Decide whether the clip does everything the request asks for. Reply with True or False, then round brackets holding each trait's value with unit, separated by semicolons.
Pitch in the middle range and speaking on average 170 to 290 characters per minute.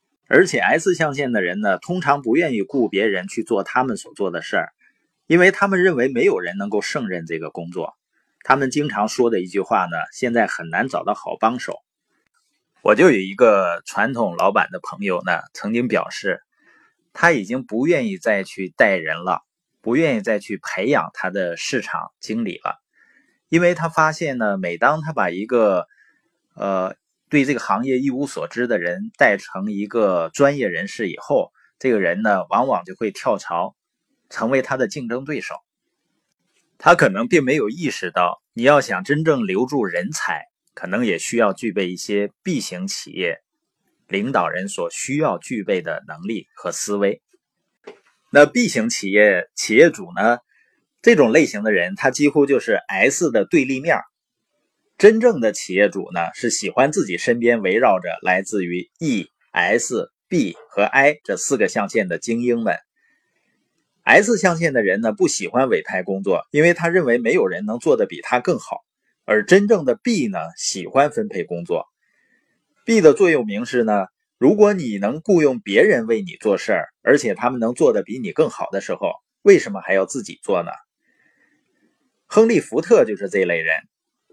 True (145 Hz; 250 characters per minute)